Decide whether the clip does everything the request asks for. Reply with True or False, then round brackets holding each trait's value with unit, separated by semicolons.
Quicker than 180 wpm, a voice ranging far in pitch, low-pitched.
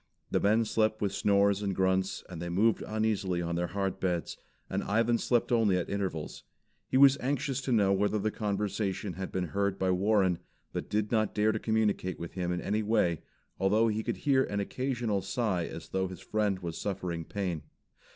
False (195 wpm; 2.7 semitones; 100 Hz)